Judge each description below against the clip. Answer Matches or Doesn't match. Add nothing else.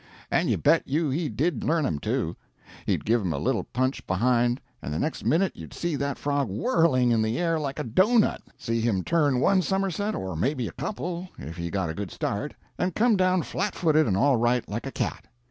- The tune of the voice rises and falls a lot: Matches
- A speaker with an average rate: Doesn't match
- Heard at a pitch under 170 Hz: Matches